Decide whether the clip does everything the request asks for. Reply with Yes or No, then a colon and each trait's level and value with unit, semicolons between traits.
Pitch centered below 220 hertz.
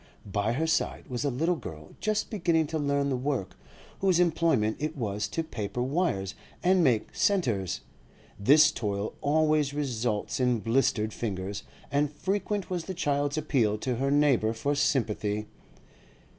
Yes: medium, 140 Hz